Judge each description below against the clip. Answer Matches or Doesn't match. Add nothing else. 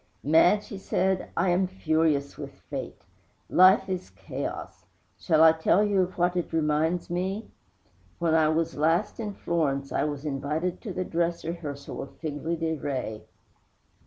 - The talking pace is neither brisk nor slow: Matches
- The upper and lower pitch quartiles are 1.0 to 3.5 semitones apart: Matches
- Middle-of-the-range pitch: Matches